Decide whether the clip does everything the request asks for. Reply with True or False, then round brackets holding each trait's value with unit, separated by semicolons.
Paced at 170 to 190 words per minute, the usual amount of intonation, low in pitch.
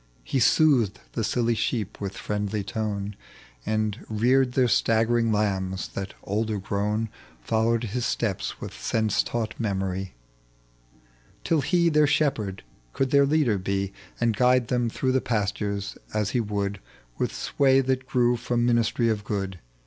False (145 wpm; 3.5 semitones; 110 Hz)